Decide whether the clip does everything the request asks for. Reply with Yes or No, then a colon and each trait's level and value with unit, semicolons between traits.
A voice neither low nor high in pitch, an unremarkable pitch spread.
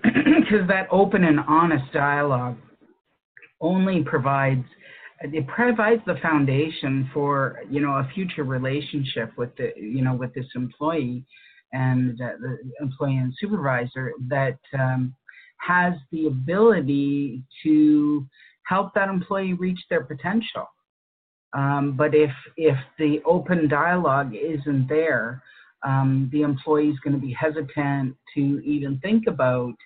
Yes: medium, 145 Hz; average, 3.5 semitones